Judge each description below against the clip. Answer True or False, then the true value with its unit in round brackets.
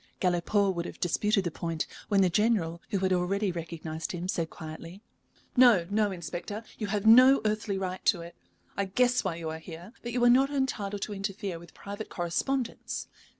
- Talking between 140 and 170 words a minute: False (190 wpm)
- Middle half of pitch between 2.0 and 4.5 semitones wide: True (3.9 semitones)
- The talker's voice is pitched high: True (195 Hz)